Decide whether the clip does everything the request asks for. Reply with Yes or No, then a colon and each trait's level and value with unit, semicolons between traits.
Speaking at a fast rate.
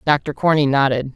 No: average, 155 wpm